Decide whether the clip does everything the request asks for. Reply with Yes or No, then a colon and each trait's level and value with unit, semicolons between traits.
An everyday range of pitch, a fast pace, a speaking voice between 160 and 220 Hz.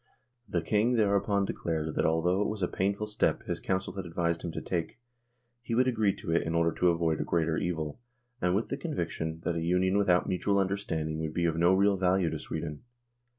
No: average, 3.3 semitones; fast, 215 wpm; very low, 90 Hz